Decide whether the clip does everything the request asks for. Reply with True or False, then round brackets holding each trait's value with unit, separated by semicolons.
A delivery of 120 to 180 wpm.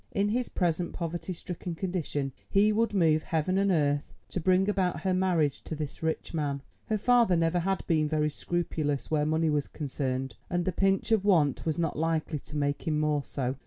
False (200 wpm)